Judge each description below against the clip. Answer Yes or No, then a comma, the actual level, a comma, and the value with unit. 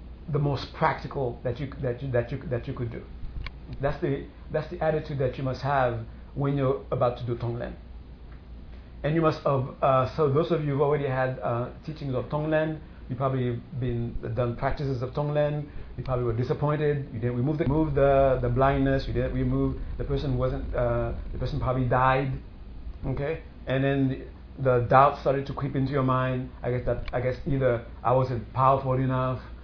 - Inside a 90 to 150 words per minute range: No, average, 195 wpm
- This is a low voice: Yes, low, 130 Hz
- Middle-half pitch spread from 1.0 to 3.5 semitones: Yes, narrow, 2.4 semitones